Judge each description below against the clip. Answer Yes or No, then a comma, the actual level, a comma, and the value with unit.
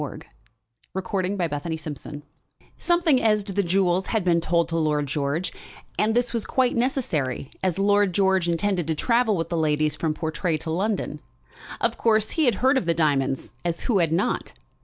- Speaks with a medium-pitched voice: Yes, medium, 180 Hz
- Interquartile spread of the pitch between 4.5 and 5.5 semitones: Yes, average, 4.9 semitones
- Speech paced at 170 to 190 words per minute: Yes, average, 185 wpm